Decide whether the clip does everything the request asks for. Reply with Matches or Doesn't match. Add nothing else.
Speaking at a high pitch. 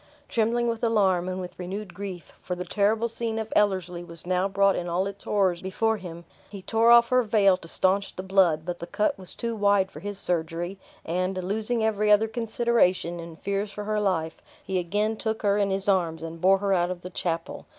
Matches